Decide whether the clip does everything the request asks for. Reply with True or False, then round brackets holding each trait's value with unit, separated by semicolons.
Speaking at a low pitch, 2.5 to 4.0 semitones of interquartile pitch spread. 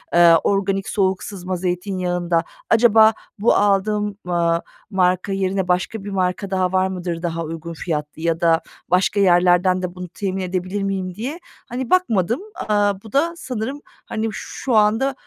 False (190 Hz; 2.8 semitones)